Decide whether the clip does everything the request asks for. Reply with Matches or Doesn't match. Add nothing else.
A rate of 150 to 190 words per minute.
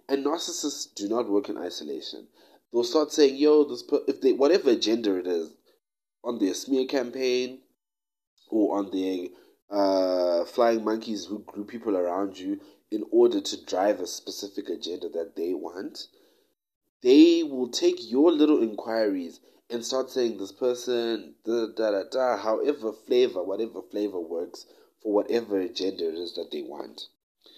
Matches